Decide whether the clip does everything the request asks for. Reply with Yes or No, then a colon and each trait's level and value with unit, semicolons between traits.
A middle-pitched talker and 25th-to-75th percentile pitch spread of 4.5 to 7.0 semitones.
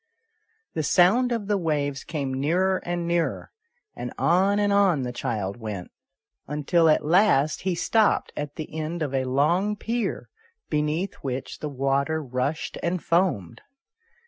Yes: medium, 160 Hz; average, 5.1 semitones